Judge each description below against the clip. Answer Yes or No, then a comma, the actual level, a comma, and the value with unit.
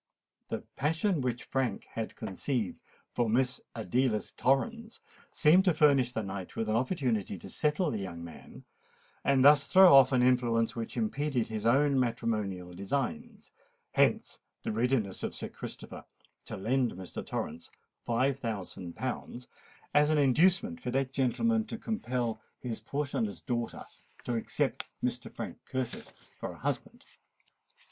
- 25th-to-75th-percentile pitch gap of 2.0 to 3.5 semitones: No, average, 4.7 semitones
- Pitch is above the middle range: No, low, 125 Hz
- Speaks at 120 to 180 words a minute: Yes, average, 145 wpm